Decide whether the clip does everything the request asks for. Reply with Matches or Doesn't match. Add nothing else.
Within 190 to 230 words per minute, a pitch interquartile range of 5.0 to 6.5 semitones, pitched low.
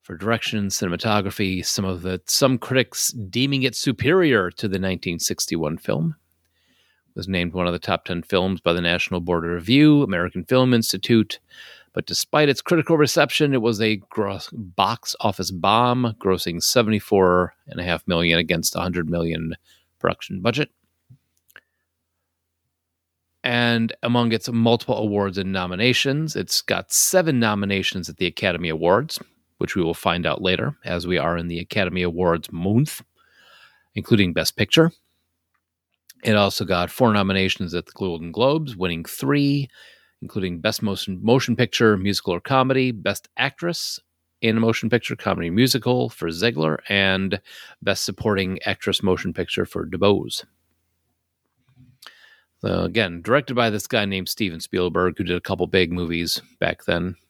Doesn't match